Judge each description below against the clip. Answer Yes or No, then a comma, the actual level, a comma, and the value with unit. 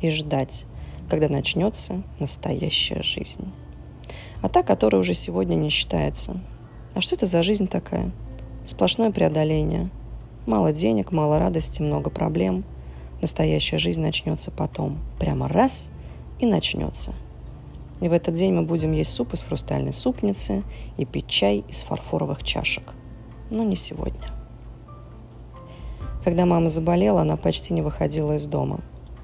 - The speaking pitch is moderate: No, low, 120 Hz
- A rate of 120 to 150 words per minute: Yes, average, 130 wpm